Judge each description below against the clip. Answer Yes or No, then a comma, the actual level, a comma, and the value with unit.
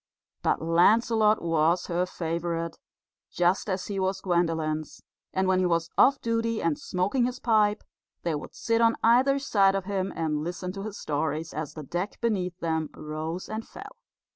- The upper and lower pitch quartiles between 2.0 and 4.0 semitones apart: No, average, 4.4 semitones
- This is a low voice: No, medium, 180 Hz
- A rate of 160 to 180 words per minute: Yes, average, 170 wpm